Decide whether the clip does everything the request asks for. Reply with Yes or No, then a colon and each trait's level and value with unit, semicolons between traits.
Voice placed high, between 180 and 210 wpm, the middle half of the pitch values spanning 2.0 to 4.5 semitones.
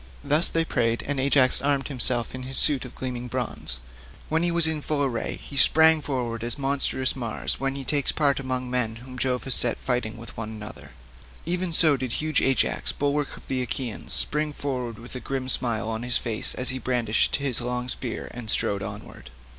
No: low, 130 Hz; average, 200 wpm; average, 3.1 semitones